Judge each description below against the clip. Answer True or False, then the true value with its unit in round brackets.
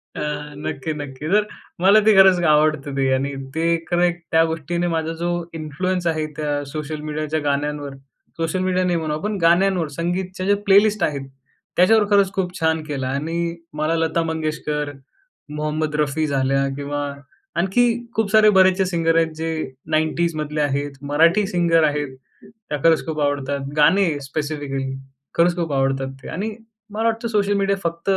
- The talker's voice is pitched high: False (160 Hz)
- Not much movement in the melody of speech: False (3.5 semitones)